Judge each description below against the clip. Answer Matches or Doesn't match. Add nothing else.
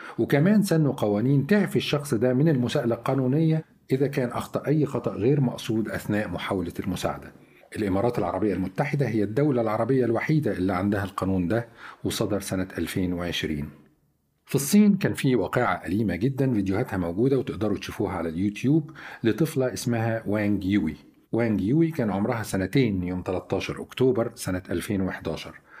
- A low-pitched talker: Matches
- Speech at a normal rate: Doesn't match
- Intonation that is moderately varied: Doesn't match